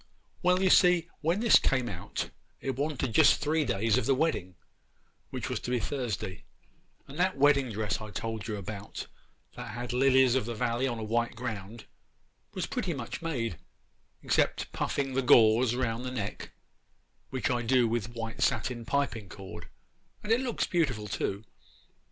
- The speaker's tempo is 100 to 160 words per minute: No, average, 170 wpm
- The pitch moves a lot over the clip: No, average, 4.0 semitones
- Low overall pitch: Yes, low, 120 Hz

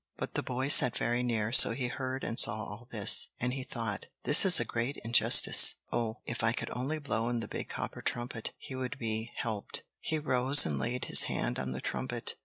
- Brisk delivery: Yes, fast, 215 wpm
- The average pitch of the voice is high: No, low, 120 Hz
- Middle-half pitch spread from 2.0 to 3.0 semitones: Yes, narrow, 2.4 semitones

